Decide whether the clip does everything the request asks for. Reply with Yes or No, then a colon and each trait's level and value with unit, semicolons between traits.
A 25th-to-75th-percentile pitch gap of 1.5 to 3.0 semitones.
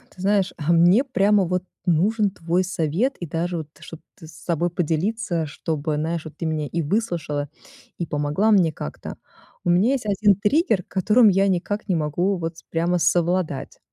No: average, 3.8 semitones